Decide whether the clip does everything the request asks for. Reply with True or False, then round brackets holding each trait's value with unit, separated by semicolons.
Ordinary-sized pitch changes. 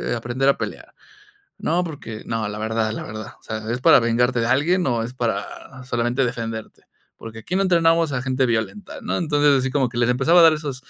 True (4.3 semitones)